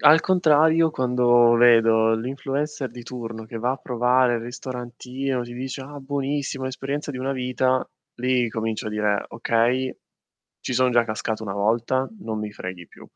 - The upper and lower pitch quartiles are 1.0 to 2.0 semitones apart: No, narrow, 2.6 semitones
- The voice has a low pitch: Yes, low, 125 Hz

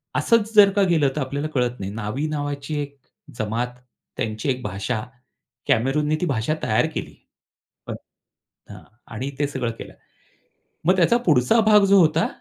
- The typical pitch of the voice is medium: Yes, medium, 145 Hz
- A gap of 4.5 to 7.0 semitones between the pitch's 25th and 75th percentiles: Yes, average, 4.8 semitones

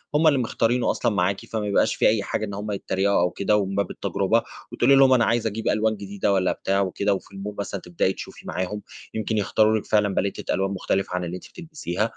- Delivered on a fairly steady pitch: Yes, narrow, 2.2 semitones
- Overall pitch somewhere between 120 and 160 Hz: No, low, 100 Hz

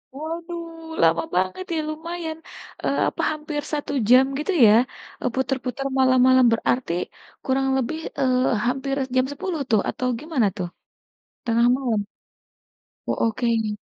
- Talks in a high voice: Yes, very high, 260 Hz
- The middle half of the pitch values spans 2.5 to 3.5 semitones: No, average, 4.3 semitones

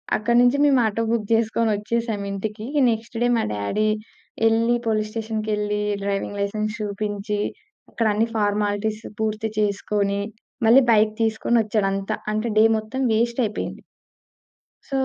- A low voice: No, high, 215 Hz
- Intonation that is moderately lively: No, narrow, 1.5 semitones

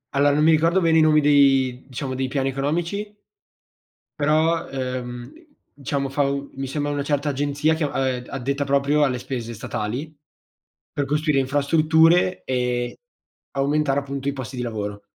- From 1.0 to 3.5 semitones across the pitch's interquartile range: Yes, narrow, 2.6 semitones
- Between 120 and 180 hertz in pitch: Yes, medium, 140 Hz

